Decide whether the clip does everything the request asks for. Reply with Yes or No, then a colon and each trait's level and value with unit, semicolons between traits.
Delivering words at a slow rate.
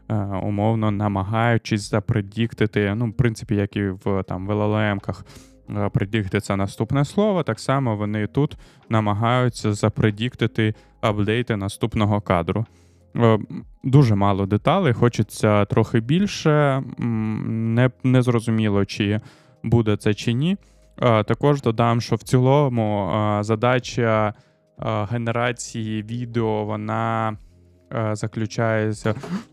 Yes: slow, 95 wpm